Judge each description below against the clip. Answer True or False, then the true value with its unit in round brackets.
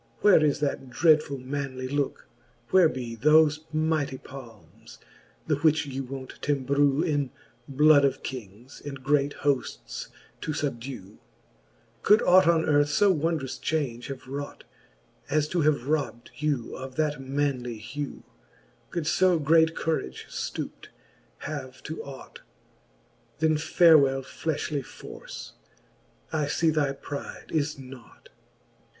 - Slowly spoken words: True (130 wpm)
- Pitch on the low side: False (145 Hz)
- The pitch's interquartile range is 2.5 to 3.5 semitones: True (2.8 semitones)